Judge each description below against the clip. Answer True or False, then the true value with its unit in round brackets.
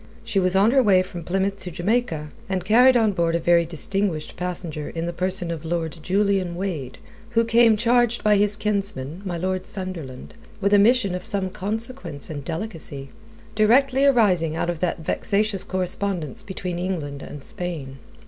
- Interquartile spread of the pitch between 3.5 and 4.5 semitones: True (3.8 semitones)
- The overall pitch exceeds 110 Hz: True (185 Hz)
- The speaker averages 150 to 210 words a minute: True (170 wpm)